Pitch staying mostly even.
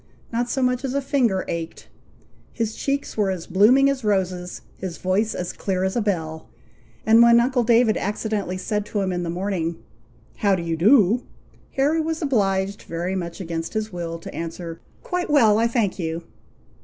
No: average, 5.1 semitones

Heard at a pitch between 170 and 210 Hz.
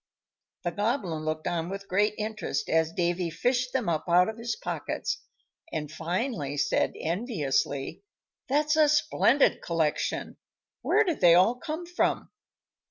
Yes: high, 190 Hz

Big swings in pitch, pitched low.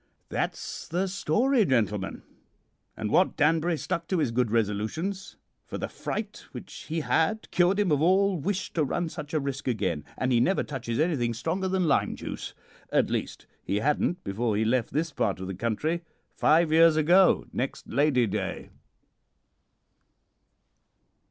No: wide, 7.1 semitones; medium, 150 Hz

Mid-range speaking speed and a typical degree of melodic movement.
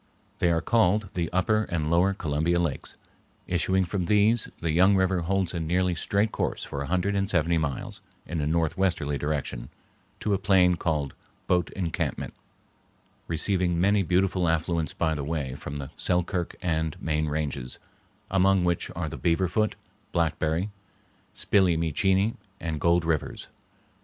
Yes: average, 155 wpm; average, 3.1 semitones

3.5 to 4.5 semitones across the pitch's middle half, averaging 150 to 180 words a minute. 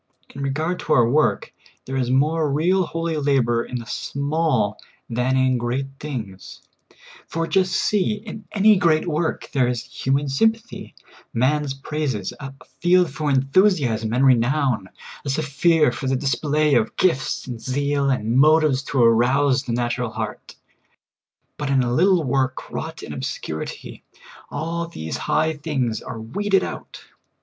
Yes: average, 4.2 semitones; average, 155 wpm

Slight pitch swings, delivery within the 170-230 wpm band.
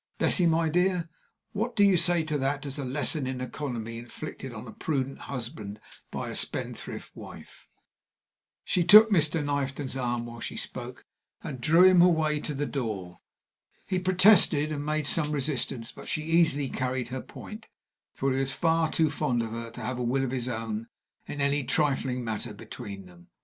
No: average, 4.8 semitones; average, 180 wpm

